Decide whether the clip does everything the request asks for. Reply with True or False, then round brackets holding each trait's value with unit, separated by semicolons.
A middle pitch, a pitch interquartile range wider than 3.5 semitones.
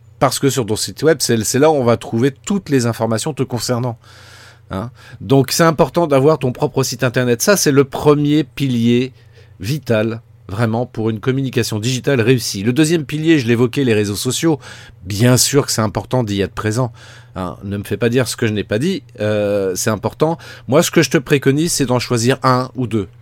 False (125 Hz; 3.9 semitones)